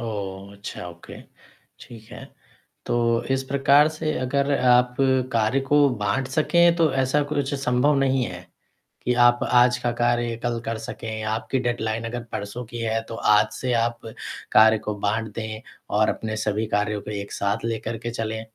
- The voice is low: Yes, low, 120 Hz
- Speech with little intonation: No, average, 3.2 semitones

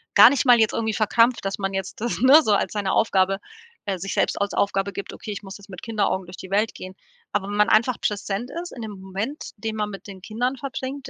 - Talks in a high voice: Yes, high, 210 Hz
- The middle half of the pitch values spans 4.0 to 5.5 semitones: No, average, 2.9 semitones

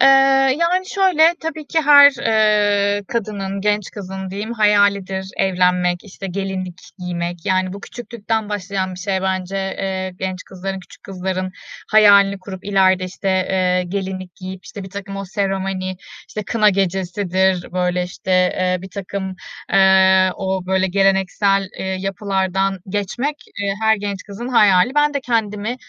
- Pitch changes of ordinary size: No, narrow, 1.6 semitones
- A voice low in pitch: No, high, 195 Hz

